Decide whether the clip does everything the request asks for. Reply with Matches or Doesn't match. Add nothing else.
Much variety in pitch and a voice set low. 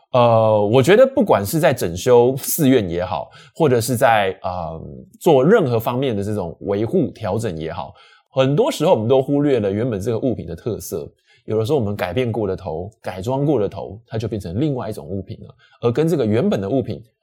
Doesn't match